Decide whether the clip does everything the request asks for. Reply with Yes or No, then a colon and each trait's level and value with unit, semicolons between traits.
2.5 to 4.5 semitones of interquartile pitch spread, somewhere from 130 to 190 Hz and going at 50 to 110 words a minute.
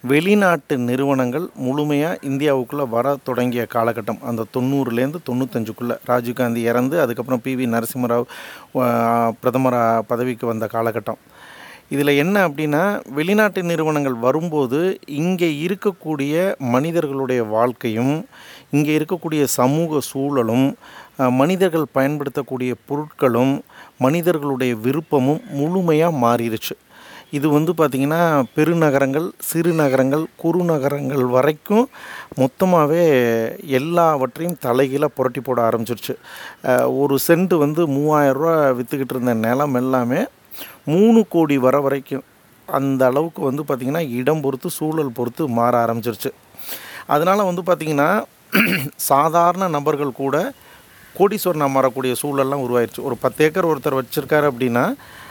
Yes: average, 3.8 semitones; medium, 140 Hz; average, 100 wpm